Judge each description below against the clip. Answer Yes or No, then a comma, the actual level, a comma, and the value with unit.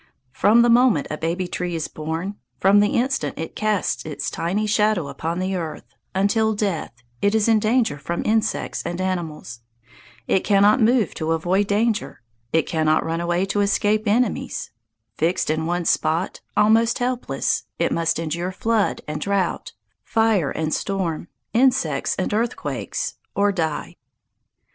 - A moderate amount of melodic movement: Yes, average, 4.7 semitones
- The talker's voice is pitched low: No, high, 195 Hz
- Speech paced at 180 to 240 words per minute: No, average, 150 wpm